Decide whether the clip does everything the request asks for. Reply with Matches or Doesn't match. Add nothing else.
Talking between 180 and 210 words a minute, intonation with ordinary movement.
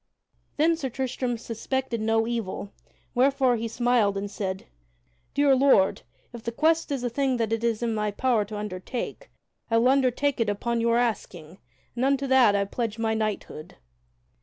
Doesn't match